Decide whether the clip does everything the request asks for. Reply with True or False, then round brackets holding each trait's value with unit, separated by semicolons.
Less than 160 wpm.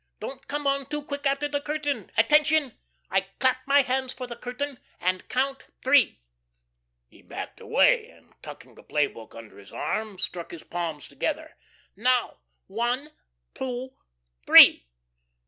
True (145 wpm)